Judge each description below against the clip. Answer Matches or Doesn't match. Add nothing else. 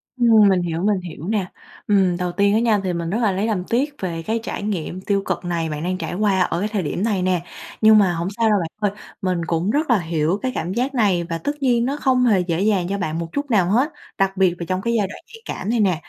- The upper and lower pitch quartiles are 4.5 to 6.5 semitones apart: Doesn't match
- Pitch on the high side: Matches